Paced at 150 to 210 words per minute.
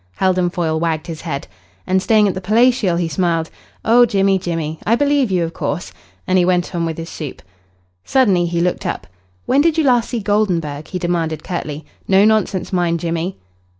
Yes: average, 190 wpm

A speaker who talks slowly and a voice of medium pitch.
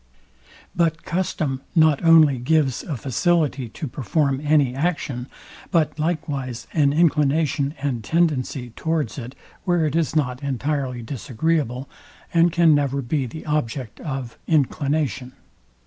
Yes: slow, 125 wpm; medium, 145 Hz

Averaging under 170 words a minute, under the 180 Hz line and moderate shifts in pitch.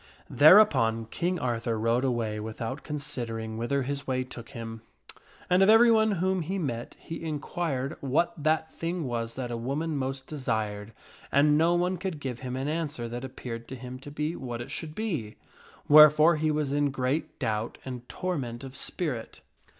No: average, 190 wpm; low, 135 Hz; average, 4.9 semitones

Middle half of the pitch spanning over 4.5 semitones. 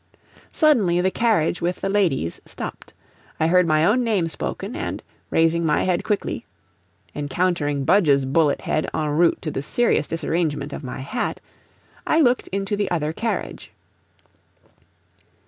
Yes: average, 4.9 semitones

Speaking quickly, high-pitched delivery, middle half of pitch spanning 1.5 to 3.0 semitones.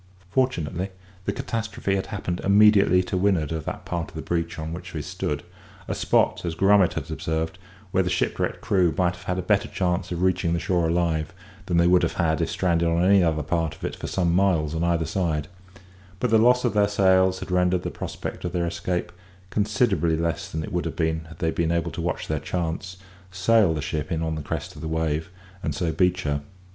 No: fast, 220 wpm; very low, 85 Hz; narrow, 2.5 semitones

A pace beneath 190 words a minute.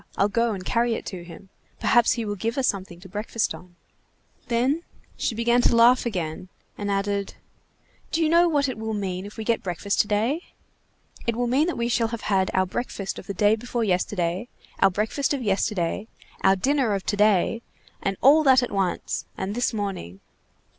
No: average, 200 wpm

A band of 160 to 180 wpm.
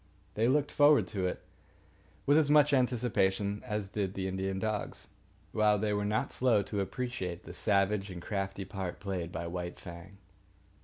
Yes: average, 165 wpm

